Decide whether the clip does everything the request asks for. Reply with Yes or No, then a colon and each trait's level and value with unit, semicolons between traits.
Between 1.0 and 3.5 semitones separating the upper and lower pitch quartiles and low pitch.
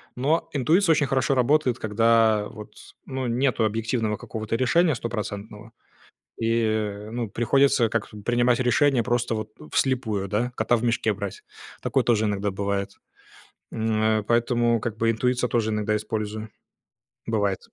Yes: narrow, 2.5 semitones; low, 115 Hz